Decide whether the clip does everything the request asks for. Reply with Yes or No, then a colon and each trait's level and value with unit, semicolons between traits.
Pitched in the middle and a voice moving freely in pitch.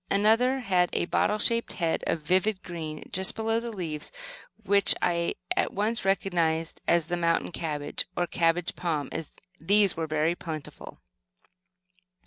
No: medium, 175 Hz; average, 3.7 semitones